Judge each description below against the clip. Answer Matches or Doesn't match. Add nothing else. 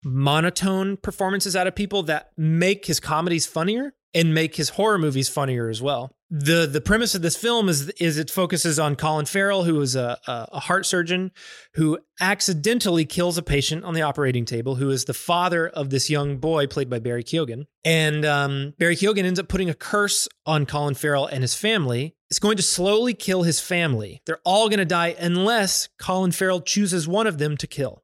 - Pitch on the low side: Doesn't match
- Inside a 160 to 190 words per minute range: Doesn't match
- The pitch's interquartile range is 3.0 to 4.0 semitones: Doesn't match